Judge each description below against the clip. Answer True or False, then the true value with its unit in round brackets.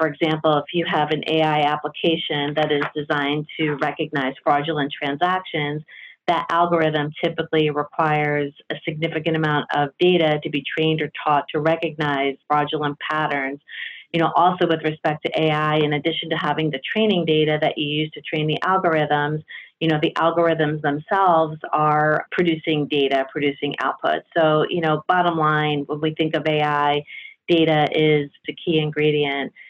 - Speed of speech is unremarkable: True (160 wpm)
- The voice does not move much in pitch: True (1.6 semitones)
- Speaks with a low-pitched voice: False (155 Hz)